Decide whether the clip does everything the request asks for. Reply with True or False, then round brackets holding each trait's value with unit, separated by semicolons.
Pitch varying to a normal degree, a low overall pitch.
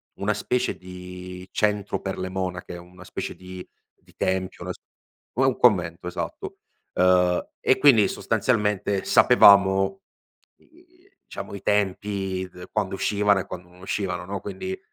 False (2.2 semitones; 95 Hz)